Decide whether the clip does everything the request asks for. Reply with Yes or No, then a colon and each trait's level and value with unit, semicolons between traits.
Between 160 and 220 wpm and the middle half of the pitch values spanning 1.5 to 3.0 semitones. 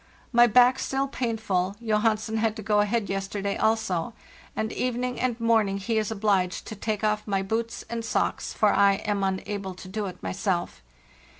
Yes: average, 170 wpm; average, 2.7 semitones